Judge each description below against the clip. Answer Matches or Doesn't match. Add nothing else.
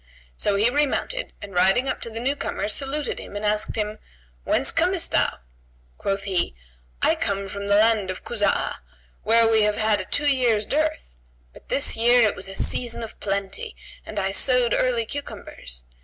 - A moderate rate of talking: Matches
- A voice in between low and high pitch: Doesn't match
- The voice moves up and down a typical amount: Matches